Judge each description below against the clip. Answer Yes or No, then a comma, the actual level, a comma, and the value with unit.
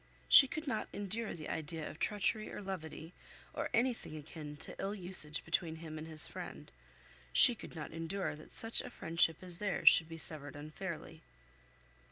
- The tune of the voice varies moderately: Yes, average, 4.2 semitones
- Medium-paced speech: Yes, average, 175 wpm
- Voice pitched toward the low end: No, medium, 165 Hz